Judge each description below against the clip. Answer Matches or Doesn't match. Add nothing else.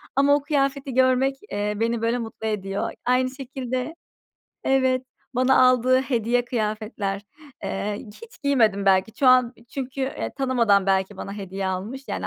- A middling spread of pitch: Matches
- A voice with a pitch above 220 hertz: Matches